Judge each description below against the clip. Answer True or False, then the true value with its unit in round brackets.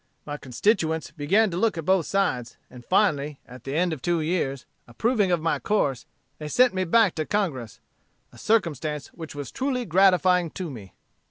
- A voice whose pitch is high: False (165 Hz)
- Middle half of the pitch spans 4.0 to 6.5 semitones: True (5.2 semitones)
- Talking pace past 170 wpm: True (180 wpm)